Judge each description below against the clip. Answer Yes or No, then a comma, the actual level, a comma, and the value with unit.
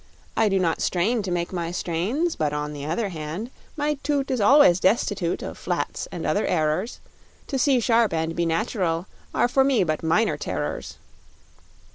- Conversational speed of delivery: Yes, average, 175 wpm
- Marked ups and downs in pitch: Yes, wide, 6.7 semitones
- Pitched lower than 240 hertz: Yes, medium, 185 Hz